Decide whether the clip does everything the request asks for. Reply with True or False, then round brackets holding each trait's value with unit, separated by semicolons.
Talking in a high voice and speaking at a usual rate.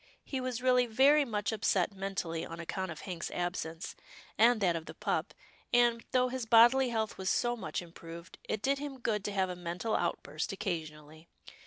True (210 Hz; 185 wpm)